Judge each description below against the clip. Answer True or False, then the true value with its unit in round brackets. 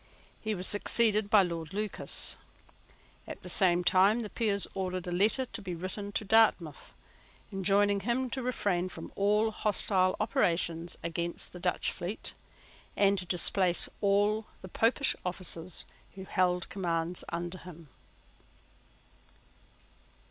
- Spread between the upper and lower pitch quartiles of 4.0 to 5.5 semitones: False (3.0 semitones)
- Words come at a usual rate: False (130 wpm)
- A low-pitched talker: False (190 Hz)